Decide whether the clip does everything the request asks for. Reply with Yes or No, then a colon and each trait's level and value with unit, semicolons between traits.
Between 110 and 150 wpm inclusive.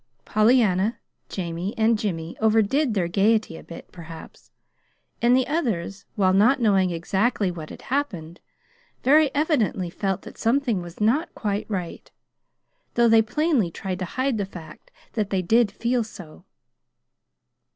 Yes: average, 140 wpm